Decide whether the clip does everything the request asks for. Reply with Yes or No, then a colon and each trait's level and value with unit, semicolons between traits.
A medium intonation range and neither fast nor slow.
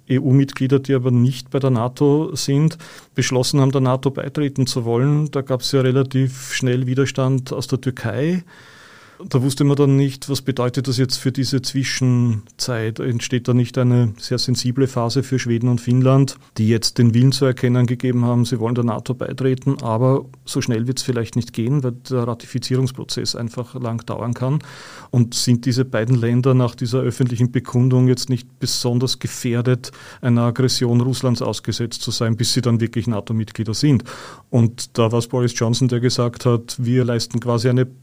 No: narrow, 1.6 semitones; average, 180 wpm